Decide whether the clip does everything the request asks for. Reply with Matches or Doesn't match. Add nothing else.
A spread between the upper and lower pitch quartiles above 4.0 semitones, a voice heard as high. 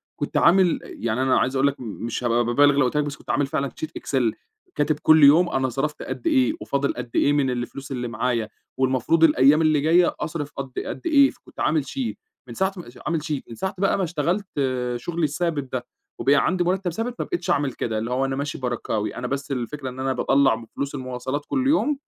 Doesn't match